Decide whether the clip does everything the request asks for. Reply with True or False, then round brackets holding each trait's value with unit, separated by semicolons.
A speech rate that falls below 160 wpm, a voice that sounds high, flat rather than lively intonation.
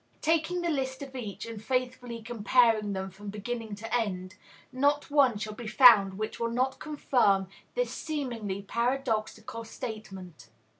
False (145 wpm; 230 Hz; 4.0 semitones)